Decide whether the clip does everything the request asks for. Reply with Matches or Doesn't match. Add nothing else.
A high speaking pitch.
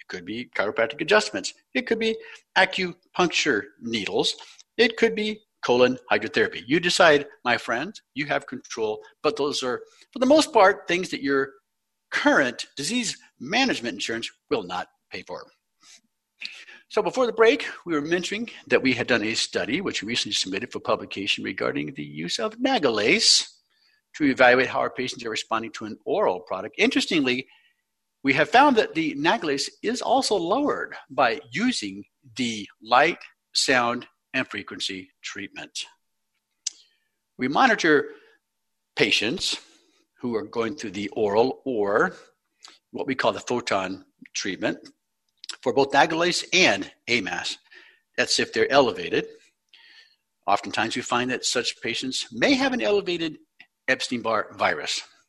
Matches